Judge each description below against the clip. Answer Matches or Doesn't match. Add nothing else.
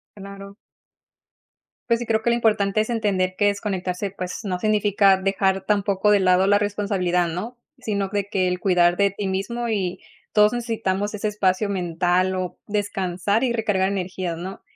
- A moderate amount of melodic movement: Doesn't match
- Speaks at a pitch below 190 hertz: Doesn't match